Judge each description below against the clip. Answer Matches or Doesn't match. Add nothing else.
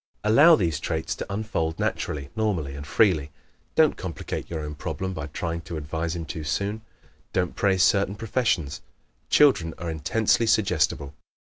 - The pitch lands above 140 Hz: Doesn't match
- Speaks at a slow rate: Doesn't match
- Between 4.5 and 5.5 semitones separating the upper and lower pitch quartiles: Matches